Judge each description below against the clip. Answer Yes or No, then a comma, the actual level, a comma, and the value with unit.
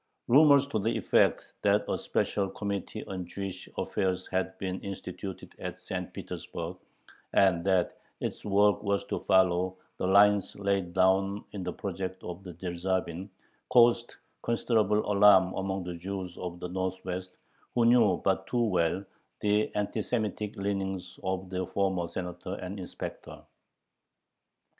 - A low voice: Yes, very low, 95 Hz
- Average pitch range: No, narrow, 1.9 semitones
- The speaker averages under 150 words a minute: Yes, average, 140 wpm